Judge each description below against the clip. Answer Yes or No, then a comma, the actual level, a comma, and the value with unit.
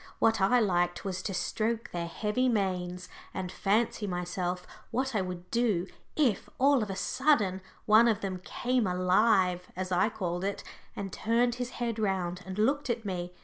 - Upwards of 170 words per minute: Yes, average, 180 wpm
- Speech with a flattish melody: No, average, 4.3 semitones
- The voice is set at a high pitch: Yes, high, 195 Hz